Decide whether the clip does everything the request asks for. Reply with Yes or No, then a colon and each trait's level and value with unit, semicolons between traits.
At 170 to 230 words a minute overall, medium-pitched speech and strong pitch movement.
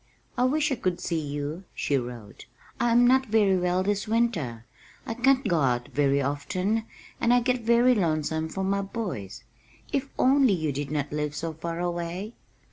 Yes: average, 180 wpm; medium, 180 Hz; wide, 8.0 semitones